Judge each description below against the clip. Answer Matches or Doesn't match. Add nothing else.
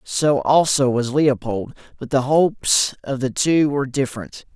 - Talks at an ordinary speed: Matches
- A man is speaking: Matches